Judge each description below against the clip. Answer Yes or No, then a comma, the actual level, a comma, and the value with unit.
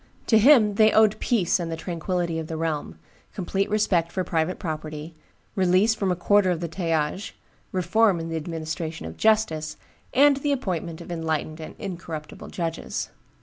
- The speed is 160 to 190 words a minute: Yes, average, 165 wpm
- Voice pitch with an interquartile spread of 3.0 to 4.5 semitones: Yes, average, 4.1 semitones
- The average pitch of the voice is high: No, medium, 175 Hz